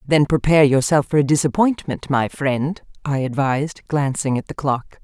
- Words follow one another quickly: No, average, 165 wpm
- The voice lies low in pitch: No, medium, 145 Hz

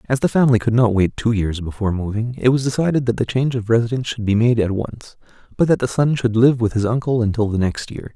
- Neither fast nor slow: No, fast, 265 wpm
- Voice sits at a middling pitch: No, low, 115 Hz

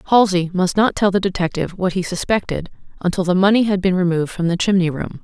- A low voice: No, medium, 185 Hz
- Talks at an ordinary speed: No, fast, 220 wpm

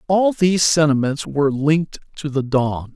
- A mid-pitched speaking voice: Yes, medium, 150 Hz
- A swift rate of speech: No, average, 165 wpm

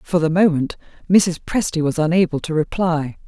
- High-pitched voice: No, medium, 165 Hz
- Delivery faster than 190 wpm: No, average, 165 wpm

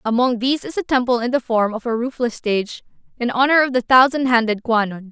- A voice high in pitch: Yes, high, 245 Hz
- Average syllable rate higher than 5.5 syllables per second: Yes, 6.0 syllables/s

